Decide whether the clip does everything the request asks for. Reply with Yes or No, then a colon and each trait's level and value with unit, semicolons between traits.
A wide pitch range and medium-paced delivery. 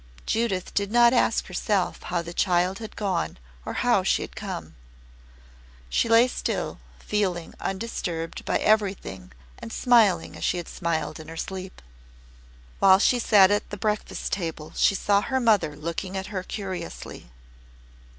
No: average, 3.5 semitones; average, 150 wpm